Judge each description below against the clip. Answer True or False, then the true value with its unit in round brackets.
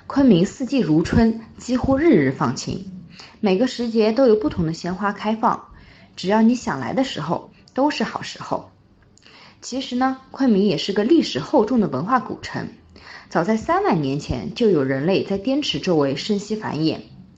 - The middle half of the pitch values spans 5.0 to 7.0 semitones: True (5.6 semitones)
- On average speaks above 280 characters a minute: False (255 characters per minute)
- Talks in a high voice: True (220 Hz)